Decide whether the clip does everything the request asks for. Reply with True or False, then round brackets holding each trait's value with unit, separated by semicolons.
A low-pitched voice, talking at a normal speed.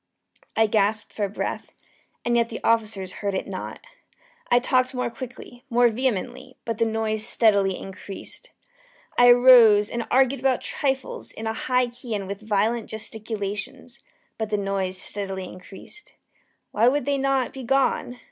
False (225 Hz; 155 wpm)